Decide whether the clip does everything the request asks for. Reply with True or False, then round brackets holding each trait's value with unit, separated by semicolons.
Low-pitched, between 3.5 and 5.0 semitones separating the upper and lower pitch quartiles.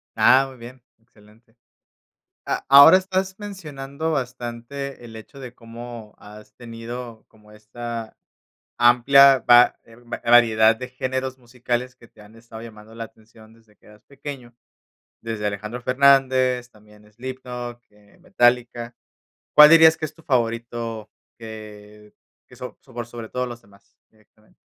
False (120 Hz; 2.7 semitones)